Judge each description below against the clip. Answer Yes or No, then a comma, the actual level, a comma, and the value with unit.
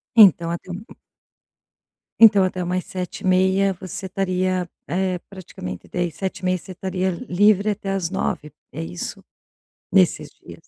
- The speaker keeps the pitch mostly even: Yes, narrow, 1.5 semitones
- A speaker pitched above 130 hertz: Yes, medium, 185 Hz